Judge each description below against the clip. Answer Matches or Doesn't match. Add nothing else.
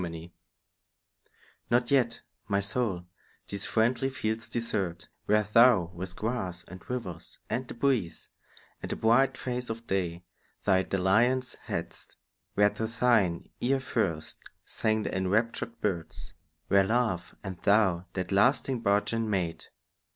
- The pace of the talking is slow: Matches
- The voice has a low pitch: Matches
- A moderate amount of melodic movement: Matches